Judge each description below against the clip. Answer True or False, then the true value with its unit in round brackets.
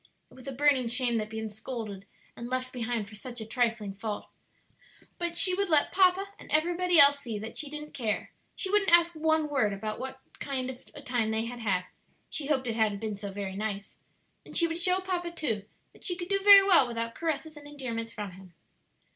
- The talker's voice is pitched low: False (255 Hz)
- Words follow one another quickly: True (220 wpm)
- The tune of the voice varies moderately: False (6.4 semitones)